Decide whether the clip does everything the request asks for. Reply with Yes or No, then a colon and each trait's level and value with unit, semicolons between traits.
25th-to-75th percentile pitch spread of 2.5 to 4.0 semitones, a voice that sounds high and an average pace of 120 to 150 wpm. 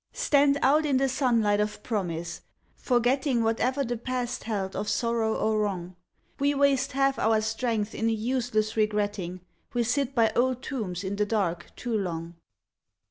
No: average, 3.7 semitones; high, 225 Hz; average, 160 wpm